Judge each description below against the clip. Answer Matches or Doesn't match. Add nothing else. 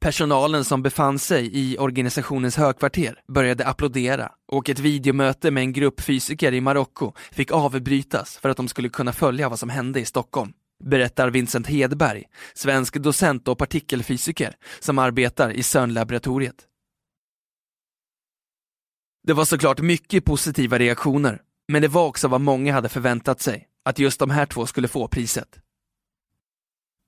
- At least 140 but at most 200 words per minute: Matches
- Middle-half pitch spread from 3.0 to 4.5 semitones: Doesn't match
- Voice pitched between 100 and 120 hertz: Doesn't match